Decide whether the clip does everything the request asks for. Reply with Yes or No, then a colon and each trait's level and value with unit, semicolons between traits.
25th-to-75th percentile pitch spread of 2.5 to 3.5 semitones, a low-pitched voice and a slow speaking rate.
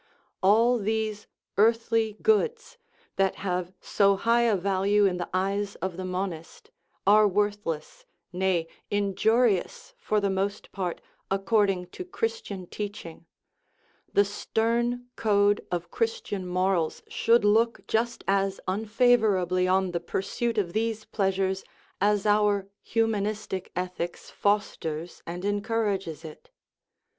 No: average, 3.0 semitones; high, 200 Hz; slow, 125 wpm